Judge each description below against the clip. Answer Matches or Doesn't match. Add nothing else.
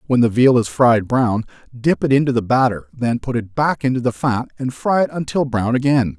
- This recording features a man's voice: Matches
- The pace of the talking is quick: Matches